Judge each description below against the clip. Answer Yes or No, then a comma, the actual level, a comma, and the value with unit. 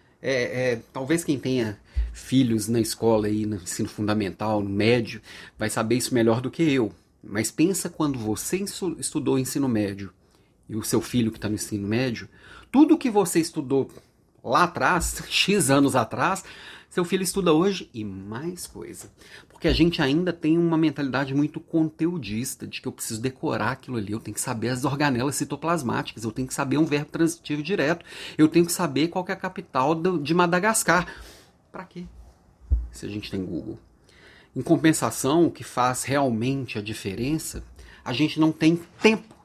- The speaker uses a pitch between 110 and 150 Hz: Yes, low, 135 Hz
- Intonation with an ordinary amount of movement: No, wide, 6.8 semitones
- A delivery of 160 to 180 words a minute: Yes, average, 175 wpm